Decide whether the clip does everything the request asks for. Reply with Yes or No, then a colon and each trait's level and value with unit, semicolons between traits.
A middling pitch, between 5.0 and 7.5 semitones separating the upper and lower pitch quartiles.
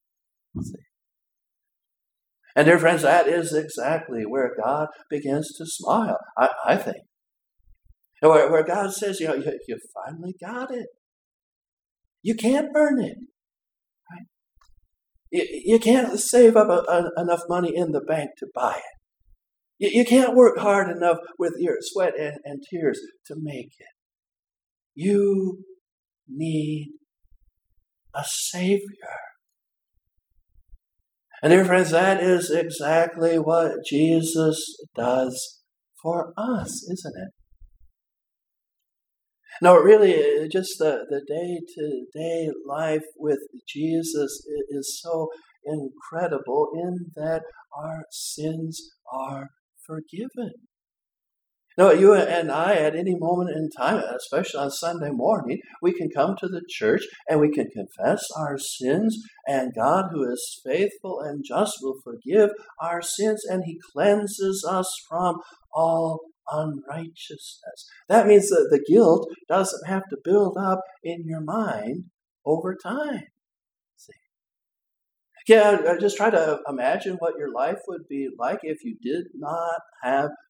Yes: medium, 170 Hz; wide, 5.5 semitones